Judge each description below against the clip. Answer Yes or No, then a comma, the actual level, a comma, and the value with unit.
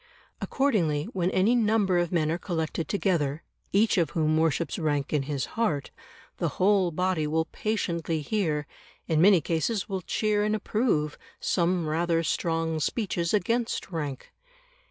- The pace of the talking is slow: No, average, 145 wpm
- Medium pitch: Yes, medium, 170 Hz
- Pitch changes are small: No, average, 4.4 semitones